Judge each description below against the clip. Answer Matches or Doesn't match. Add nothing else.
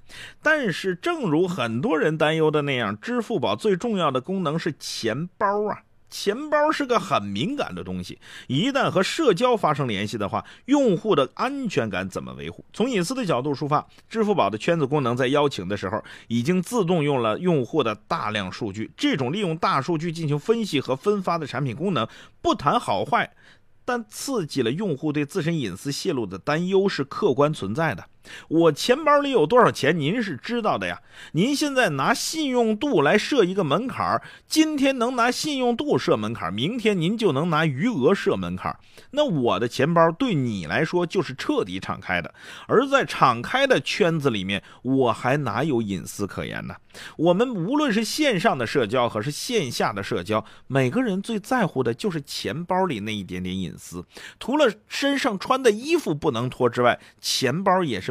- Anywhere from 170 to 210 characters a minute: Doesn't match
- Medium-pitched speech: Matches